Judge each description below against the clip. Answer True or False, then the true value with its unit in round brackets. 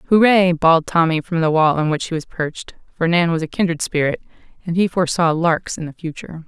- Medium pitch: True (165 Hz)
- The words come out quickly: True (220 wpm)